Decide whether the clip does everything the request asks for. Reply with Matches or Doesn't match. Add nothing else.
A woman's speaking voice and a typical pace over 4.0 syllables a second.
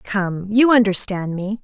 Doesn't match